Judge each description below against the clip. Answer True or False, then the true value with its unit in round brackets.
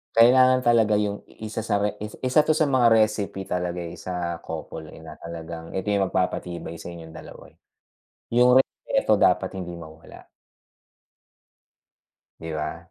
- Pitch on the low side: True (95 Hz)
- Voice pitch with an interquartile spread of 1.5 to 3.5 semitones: False (5.1 semitones)